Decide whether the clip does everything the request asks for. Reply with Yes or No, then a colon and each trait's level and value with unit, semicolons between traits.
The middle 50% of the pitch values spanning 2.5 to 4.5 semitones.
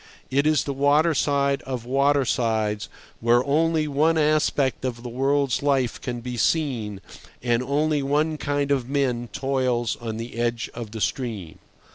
Yes: average, 3.3 semitones